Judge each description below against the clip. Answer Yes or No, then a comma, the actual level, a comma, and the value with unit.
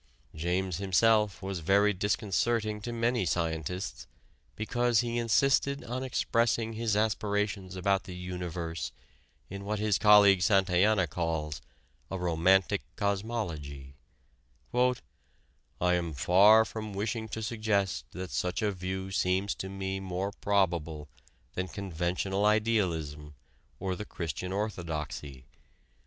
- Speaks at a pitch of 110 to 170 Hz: No, very low, 95 Hz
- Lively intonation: No, average, 3.3 semitones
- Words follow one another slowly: Yes, slow, 115 wpm